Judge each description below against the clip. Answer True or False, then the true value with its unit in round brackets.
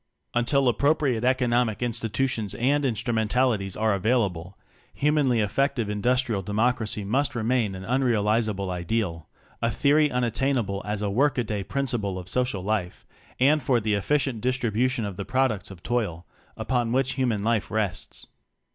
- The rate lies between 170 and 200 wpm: False (155 wpm)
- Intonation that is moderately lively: True (3.9 semitones)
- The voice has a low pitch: True (115 Hz)